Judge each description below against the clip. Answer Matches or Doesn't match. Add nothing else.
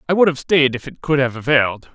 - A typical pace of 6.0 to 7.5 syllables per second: Matches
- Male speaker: Matches